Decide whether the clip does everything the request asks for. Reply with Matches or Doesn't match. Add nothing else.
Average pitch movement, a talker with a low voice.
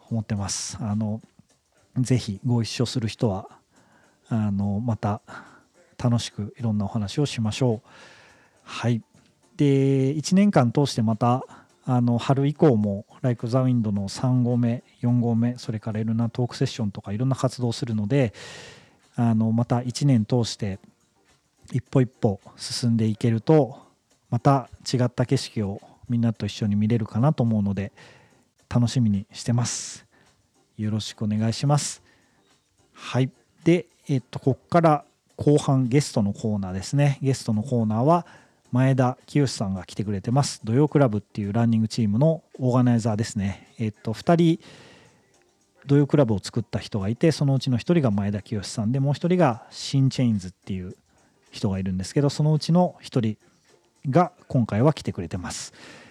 Matches